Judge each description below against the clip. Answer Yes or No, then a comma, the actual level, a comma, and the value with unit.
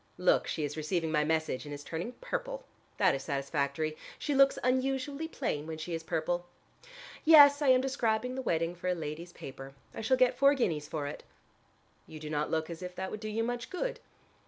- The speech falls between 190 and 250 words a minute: Yes, fast, 205 wpm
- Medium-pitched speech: Yes, medium, 175 Hz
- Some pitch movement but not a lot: No, wide, 8.9 semitones